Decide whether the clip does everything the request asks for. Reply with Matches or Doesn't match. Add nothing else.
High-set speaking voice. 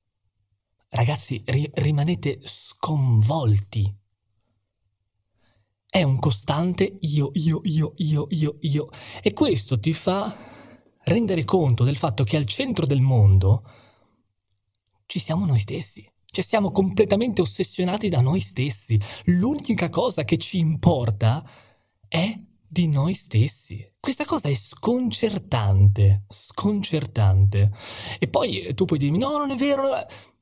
Doesn't match